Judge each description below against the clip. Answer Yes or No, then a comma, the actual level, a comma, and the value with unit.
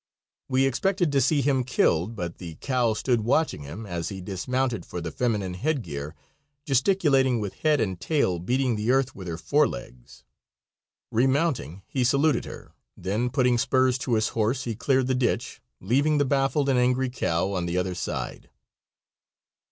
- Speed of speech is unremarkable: Yes, average, 170 wpm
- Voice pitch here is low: Yes, low, 125 Hz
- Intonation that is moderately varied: No, wide, 6.2 semitones